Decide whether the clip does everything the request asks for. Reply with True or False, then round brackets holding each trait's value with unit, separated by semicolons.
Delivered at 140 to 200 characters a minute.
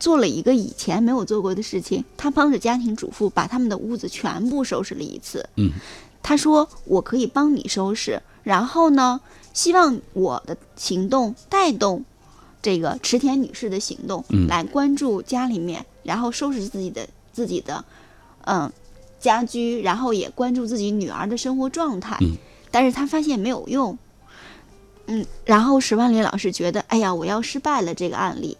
False (260 characters per minute)